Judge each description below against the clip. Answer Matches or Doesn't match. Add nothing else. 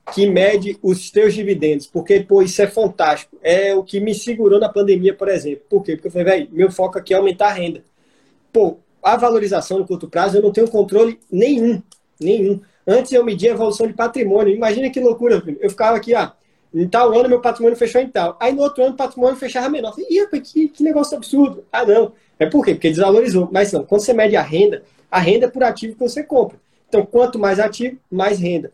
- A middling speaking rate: Doesn't match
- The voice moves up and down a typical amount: Matches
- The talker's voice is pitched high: Matches